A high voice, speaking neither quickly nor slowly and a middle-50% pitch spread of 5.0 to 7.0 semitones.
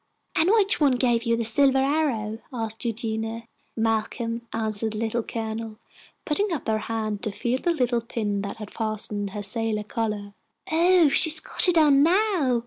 No: high, 230 Hz; average, 165 wpm; average, 4.3 semitones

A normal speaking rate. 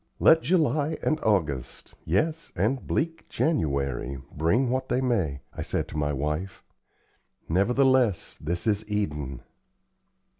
No: slow, 120 wpm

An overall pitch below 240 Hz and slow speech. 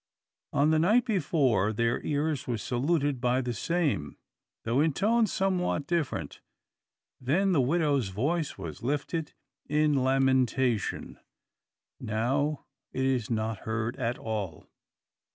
Yes: low, 135 Hz; slow, 120 wpm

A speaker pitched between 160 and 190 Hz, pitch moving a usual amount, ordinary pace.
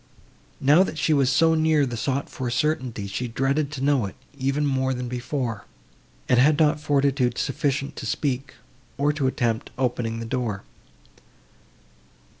No: low, 135 Hz; average, 3.0 semitones; average, 155 wpm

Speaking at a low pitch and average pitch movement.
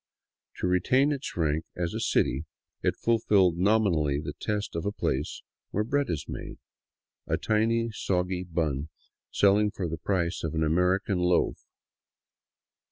Yes: very low, 90 Hz; average, 4.4 semitones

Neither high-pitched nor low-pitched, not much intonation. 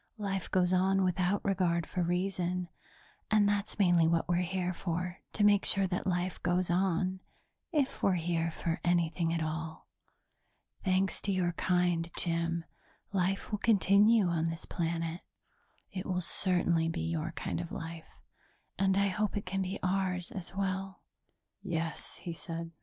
Yes: medium, 180 Hz; narrow, 2.3 semitones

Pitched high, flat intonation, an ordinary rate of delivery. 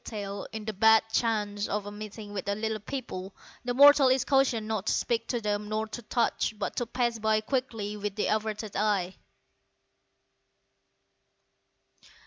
Yes: high, 215 Hz; narrow, 2.1 semitones; average, 155 wpm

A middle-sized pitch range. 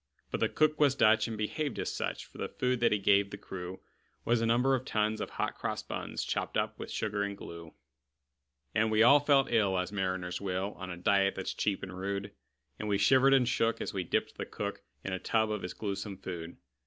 Yes: average, 3.5 semitones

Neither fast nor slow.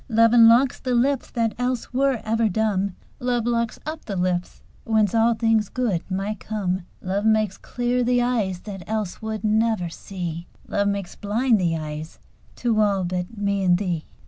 Yes: average, 170 wpm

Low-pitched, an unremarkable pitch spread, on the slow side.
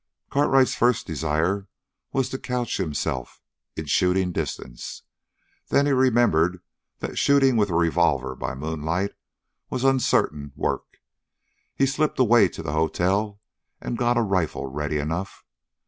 No: very low, 95 Hz; wide, 7.7 semitones; slow, 130 wpm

